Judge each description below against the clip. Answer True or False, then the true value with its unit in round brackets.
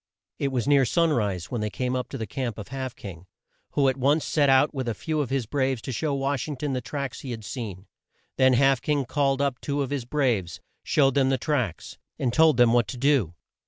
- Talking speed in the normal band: False (235 wpm)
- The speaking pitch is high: False (130 Hz)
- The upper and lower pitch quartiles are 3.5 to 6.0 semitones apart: False (3.0 semitones)